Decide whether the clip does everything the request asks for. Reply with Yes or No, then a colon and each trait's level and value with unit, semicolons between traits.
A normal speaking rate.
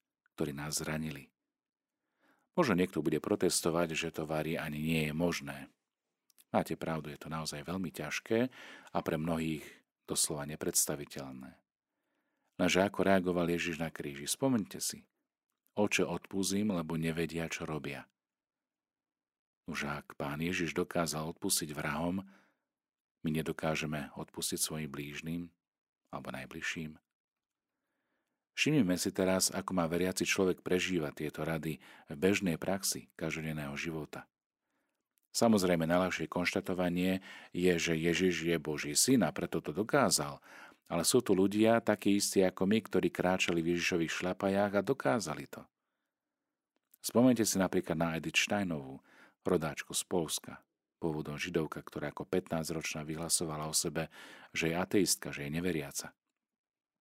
Yes: average, 125 wpm